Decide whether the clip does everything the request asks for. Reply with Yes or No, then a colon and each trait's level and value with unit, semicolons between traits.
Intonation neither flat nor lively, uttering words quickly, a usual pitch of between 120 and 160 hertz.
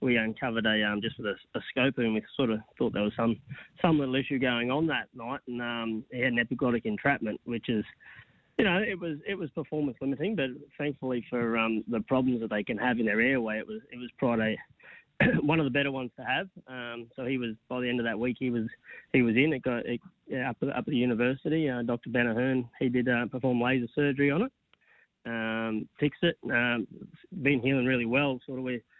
Yes: average, 3.1 semitones; fast, 230 wpm; low, 125 Hz